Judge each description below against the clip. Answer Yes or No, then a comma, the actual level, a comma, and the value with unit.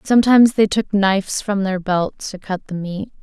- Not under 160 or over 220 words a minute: Yes, fast, 205 wpm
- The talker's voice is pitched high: Yes, high, 200 Hz